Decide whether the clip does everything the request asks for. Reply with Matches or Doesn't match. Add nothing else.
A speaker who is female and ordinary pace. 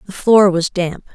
Doesn't match